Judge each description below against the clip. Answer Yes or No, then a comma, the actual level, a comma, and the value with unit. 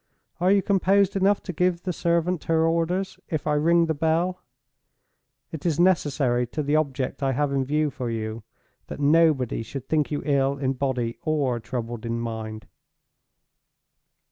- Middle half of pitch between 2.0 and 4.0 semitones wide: No, average, 4.7 semitones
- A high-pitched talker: No, medium, 150 Hz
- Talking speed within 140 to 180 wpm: Yes, average, 165 wpm